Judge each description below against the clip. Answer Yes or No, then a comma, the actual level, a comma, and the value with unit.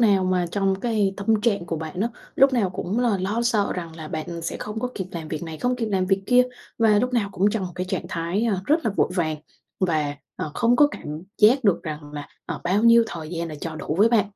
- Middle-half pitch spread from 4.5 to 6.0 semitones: Yes, average, 5.0 semitones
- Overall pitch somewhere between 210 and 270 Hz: No, high, 195 Hz